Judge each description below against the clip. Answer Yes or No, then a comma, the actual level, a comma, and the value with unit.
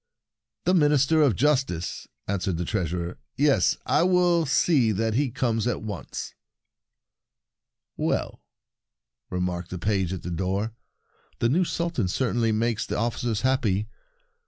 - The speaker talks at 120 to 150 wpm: Yes, slow, 135 wpm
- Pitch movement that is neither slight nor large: No, wide, 6.9 semitones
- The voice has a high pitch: No, low, 115 Hz